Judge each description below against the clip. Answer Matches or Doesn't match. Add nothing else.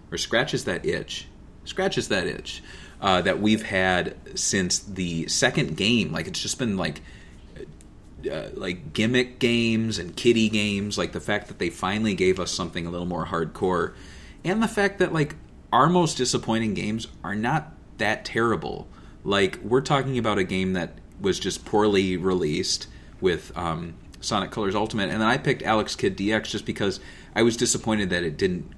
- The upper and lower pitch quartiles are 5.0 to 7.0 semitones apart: Doesn't match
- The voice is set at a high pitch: Doesn't match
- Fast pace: Doesn't match